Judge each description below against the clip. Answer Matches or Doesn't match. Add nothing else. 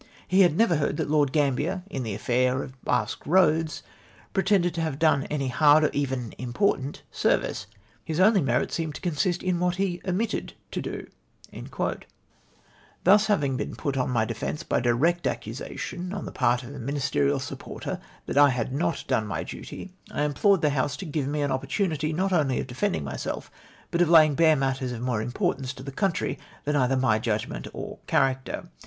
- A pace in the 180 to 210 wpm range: Matches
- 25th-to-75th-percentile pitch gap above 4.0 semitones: Matches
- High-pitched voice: Doesn't match